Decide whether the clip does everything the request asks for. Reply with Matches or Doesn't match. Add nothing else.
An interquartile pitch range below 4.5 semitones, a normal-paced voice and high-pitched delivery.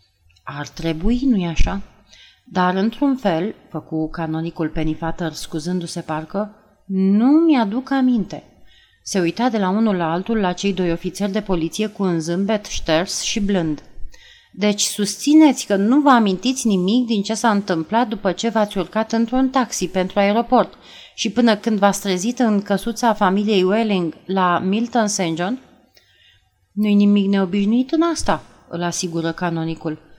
Doesn't match